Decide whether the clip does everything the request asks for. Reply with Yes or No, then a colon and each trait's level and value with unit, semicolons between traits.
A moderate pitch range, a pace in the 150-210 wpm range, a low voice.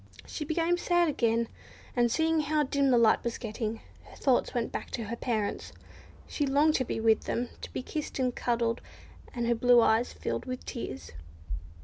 No: average, 4.0 semitones; average, 190 wpm; high, 245 Hz